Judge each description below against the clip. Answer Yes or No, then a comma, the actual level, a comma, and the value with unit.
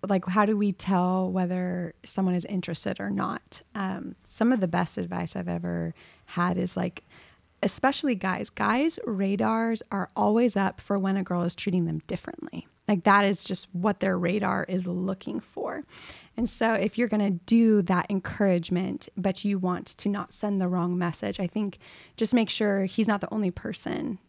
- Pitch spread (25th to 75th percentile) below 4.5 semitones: Yes, average, 2.8 semitones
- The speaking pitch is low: No, high, 195 Hz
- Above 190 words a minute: No, average, 185 wpm